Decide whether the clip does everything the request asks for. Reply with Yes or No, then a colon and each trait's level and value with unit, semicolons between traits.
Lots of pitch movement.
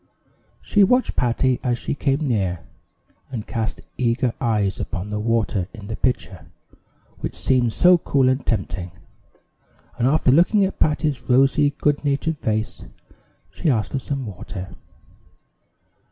No: average, 4.8 semitones